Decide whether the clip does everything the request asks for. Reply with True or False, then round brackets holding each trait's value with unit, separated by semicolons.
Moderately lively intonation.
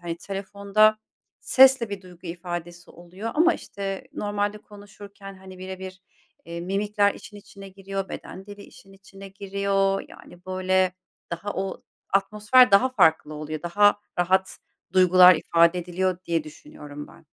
False (2.3 semitones)